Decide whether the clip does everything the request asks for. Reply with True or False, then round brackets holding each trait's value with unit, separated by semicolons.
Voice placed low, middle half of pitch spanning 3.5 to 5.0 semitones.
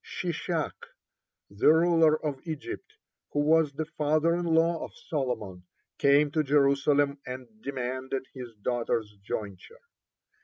False (145 Hz; 3.8 semitones)